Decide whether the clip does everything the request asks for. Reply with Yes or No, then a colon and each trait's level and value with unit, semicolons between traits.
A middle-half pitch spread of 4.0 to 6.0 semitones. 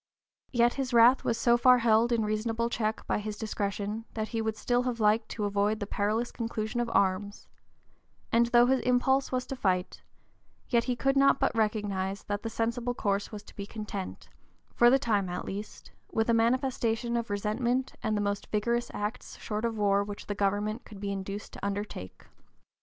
No: average, 2.7 semitones